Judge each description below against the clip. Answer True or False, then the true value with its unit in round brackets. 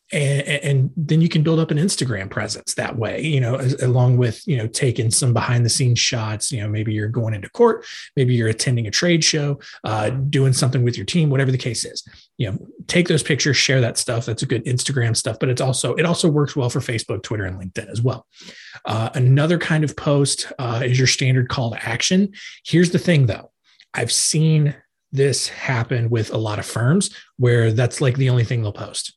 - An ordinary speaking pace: False (220 wpm)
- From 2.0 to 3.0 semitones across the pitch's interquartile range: False (3.9 semitones)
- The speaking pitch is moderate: False (130 Hz)